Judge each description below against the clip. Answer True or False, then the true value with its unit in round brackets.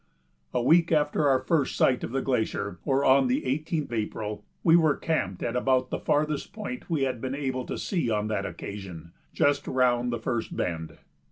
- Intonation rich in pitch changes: False (4.7 semitones)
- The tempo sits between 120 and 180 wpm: False (190 wpm)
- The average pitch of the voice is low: True (130 Hz)